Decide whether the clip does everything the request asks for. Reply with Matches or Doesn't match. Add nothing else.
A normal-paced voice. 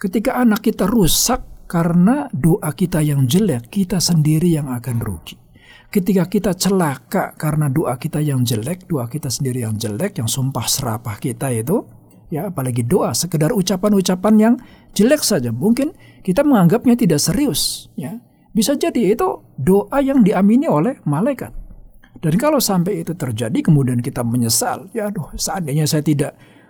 Doesn't match